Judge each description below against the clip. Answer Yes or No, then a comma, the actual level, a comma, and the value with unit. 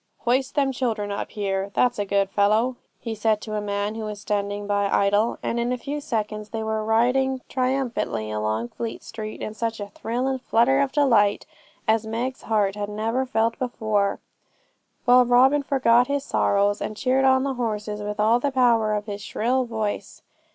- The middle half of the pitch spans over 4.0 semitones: No, average, 3.4 semitones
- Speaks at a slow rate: No, average, 190 wpm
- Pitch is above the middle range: Yes, high, 225 Hz